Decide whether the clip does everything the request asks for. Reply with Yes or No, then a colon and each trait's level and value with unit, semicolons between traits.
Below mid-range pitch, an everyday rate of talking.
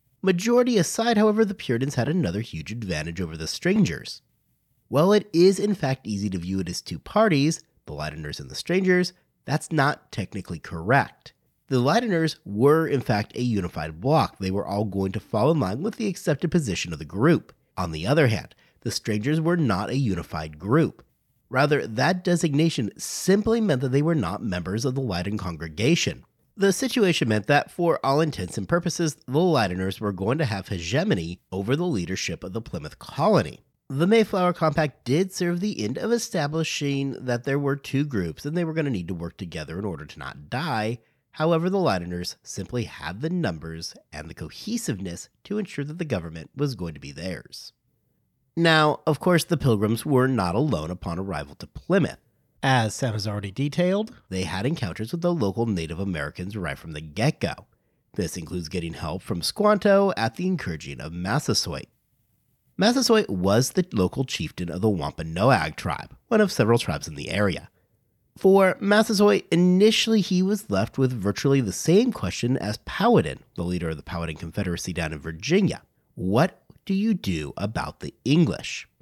Yes: low, 130 Hz; average, 180 wpm